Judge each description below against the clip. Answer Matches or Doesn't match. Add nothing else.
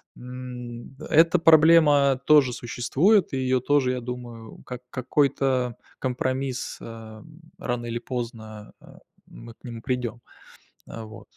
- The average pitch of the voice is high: Doesn't match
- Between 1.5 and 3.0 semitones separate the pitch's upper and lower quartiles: Matches